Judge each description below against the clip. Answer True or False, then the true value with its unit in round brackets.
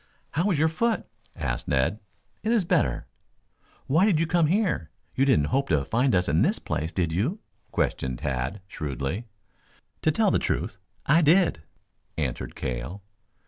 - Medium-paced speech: True (160 wpm)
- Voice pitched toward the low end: True (100 Hz)